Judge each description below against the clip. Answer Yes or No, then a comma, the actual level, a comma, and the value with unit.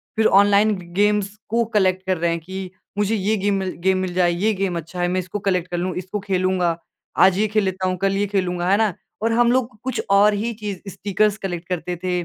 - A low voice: No, high, 190 Hz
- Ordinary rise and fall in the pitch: No, narrow, 2.3 semitones